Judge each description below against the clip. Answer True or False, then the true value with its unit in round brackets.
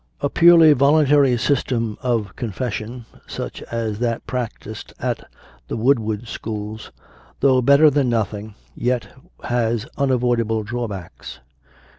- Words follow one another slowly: True (115 wpm)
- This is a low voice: True (120 Hz)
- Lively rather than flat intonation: False (3.0 semitones)